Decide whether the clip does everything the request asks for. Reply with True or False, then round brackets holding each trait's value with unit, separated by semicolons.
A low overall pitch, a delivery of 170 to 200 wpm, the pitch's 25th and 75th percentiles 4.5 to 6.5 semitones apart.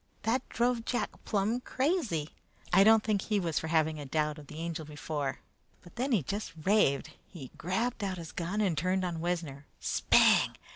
False (180 Hz; 185 wpm; 5.5 semitones)